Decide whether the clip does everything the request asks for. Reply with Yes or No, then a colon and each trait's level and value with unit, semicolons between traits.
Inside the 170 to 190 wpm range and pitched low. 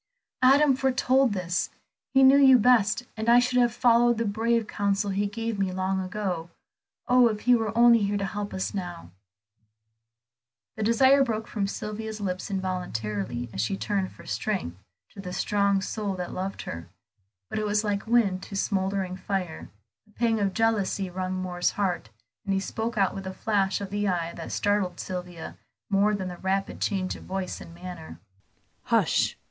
No: average, 175 wpm; high, 200 Hz